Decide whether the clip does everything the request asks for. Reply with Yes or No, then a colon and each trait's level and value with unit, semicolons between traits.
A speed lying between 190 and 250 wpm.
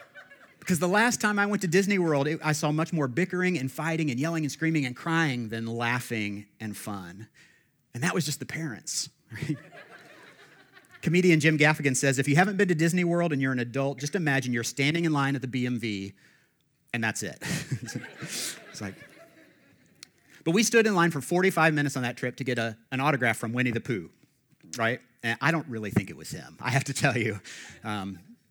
Yes: fast, 205 wpm